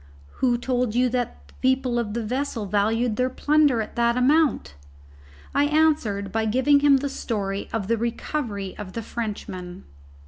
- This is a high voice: Yes, high, 235 Hz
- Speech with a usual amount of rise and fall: Yes, average, 3.7 semitones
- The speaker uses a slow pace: No, average, 165 wpm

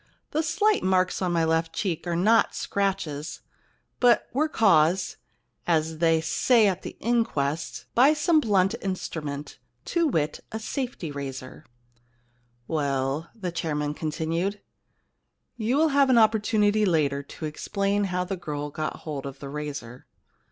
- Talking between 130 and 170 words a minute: Yes, average, 155 wpm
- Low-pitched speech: No, medium, 170 Hz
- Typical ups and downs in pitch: No, wide, 6.5 semitones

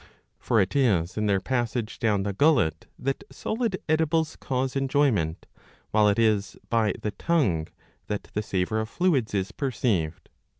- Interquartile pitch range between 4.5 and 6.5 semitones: Yes, wide, 5.5 semitones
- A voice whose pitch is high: No, low, 110 Hz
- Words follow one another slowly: No, average, 160 wpm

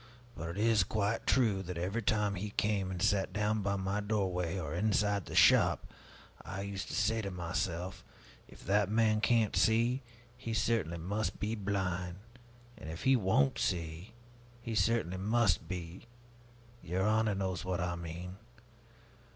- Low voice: Yes, low, 100 Hz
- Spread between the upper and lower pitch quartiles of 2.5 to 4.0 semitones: Yes, average, 3.2 semitones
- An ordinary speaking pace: Yes, average, 160 wpm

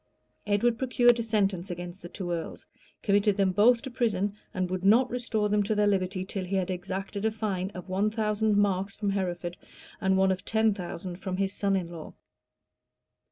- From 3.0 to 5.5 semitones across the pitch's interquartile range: No, narrow, 2.5 semitones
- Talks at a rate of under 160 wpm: No, average, 195 wpm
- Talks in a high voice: Yes, high, 195 Hz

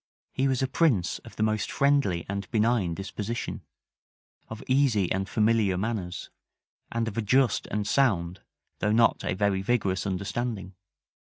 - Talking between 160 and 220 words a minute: No, average, 150 wpm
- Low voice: Yes, low, 105 Hz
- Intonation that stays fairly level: No, average, 3.7 semitones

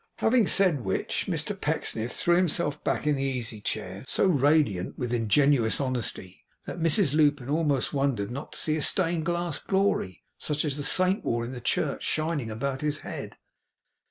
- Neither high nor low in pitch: Yes, medium, 145 Hz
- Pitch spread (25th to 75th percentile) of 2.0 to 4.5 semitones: No, average, 5.2 semitones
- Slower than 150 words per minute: No, average, 175 wpm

